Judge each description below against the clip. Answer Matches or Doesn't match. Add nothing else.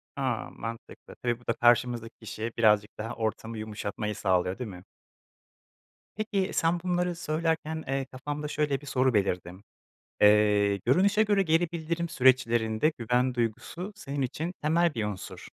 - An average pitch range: Doesn't match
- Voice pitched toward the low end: Matches